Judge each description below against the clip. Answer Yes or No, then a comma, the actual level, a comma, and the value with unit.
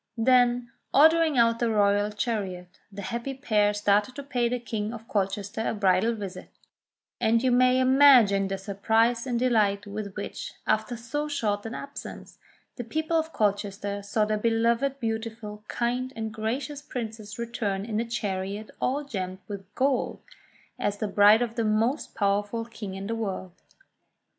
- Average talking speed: Yes, average, 160 wpm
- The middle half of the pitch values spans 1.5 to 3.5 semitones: Yes, average, 3.1 semitones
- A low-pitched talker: No, high, 225 Hz